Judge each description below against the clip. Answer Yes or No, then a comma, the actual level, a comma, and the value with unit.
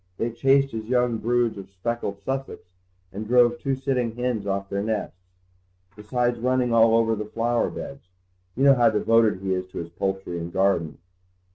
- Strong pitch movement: No, average, 3.8 semitones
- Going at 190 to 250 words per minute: No, average, 175 wpm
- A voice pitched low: Yes, low, 115 Hz